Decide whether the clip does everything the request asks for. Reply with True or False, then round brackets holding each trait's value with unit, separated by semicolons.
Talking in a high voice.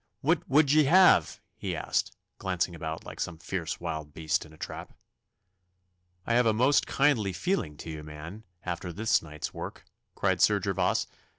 False (90 Hz)